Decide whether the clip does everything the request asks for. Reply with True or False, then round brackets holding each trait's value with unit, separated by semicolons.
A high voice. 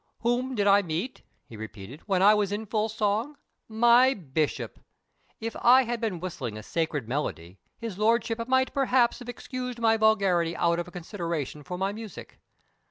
True (205 Hz)